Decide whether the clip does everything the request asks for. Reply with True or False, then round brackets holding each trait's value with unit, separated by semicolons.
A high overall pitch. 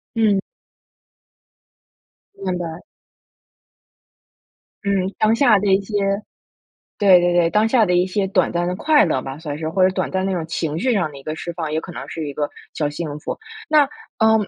False (180 Hz)